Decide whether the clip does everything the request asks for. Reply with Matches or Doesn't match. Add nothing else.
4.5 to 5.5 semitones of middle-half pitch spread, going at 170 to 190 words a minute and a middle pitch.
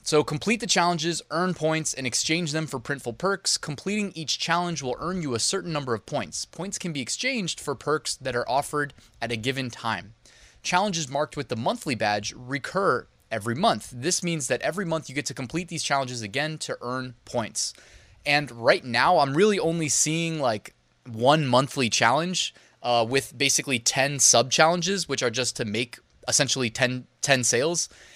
Matches